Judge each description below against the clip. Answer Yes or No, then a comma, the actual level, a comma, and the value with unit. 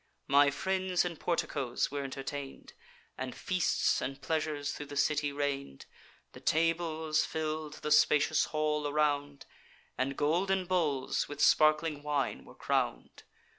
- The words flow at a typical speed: No, slow, 130 wpm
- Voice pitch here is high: No, medium, 150 Hz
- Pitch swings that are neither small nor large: No, narrow, 2.0 semitones